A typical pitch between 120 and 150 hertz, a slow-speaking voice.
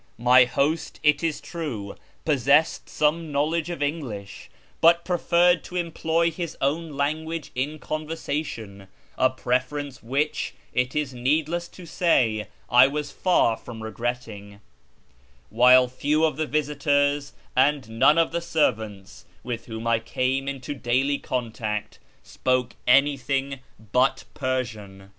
Yes: medium, 140 Hz; slow, 130 wpm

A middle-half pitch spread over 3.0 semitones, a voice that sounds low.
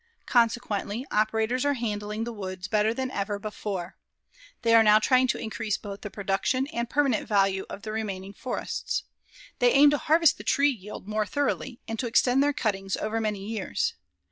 No: average, 3.5 semitones; high, 220 Hz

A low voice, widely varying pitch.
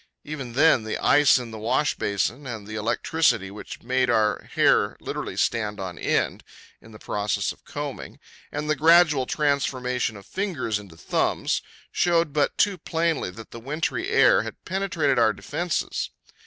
Yes: low, 130 Hz; wide, 5.9 semitones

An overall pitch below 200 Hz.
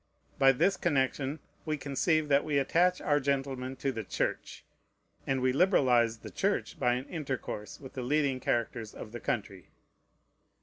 Yes: low, 135 Hz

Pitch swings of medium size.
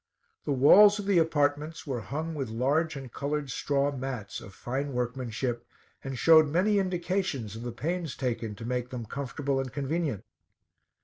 Yes: average, 4.4 semitones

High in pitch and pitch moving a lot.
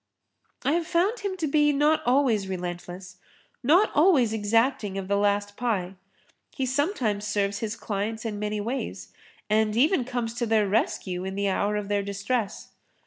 No: high, 220 Hz; average, 4.8 semitones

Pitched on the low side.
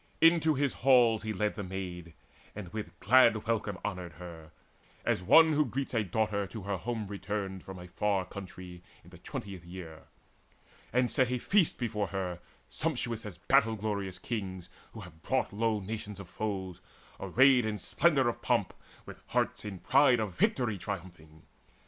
Yes: low, 105 Hz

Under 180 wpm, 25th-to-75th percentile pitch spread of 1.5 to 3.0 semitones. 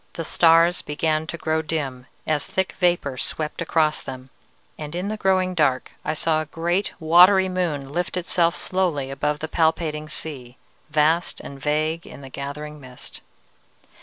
Yes: average, 160 wpm; average, 2.7 semitones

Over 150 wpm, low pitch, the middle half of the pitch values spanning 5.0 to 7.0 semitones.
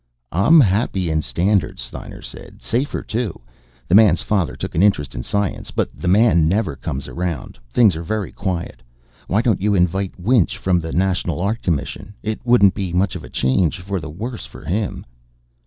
No: average, 185 wpm; very low, 95 Hz; average, 3.9 semitones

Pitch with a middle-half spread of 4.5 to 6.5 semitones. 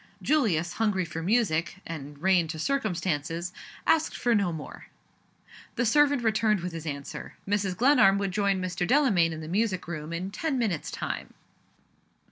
Yes: average, 5.2 semitones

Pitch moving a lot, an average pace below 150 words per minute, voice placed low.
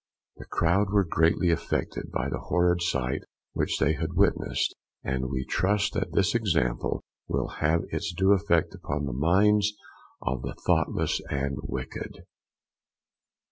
Yes: wide, 5.9 semitones; average, 140 wpm; very low, 85 Hz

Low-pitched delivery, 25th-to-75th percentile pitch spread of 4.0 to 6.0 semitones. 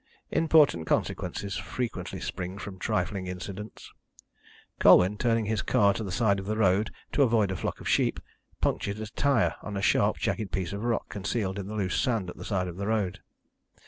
No: low, 100 Hz; average, 2.8 semitones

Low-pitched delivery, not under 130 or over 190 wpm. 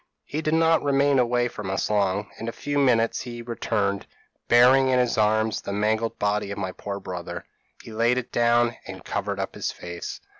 No: low, 115 Hz; average, 200 wpm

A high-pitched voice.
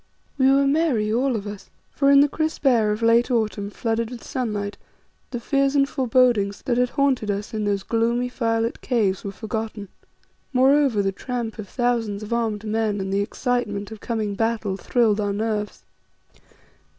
Yes: high, 225 Hz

